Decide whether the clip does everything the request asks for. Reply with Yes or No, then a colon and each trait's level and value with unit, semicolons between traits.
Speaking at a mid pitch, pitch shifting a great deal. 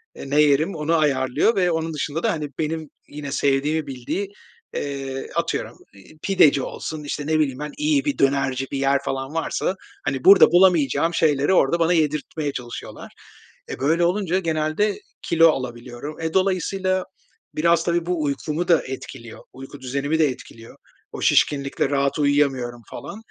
No: medium, 150 Hz; average, 3.5 semitones